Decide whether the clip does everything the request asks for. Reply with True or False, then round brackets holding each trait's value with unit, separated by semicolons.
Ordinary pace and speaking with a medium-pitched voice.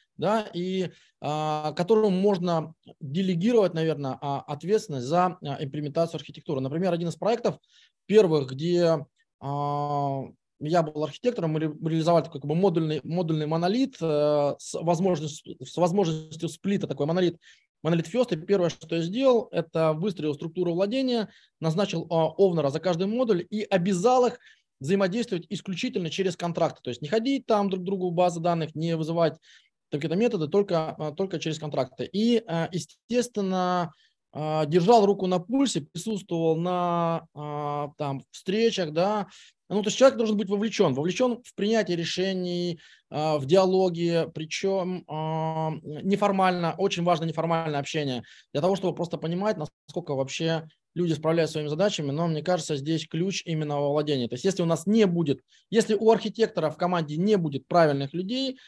True (145 wpm; 170 Hz)